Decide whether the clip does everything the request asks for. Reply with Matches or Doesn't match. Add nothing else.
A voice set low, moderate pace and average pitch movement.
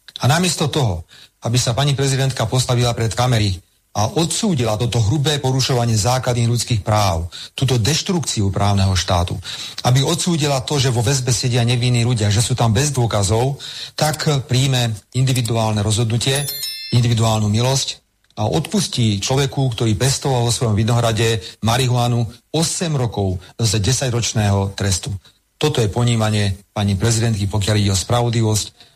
Matches